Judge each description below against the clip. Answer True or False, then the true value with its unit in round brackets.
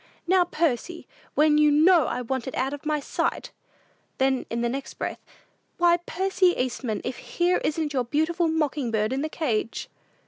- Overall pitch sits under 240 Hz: False (295 Hz)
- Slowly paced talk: False (175 wpm)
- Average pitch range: True (4.7 semitones)